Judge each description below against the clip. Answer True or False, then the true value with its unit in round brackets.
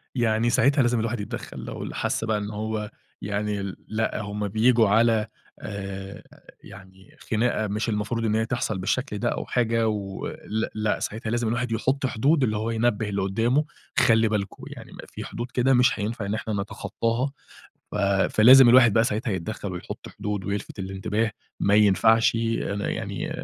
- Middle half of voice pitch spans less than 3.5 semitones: True (2.4 semitones)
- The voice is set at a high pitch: False (110 Hz)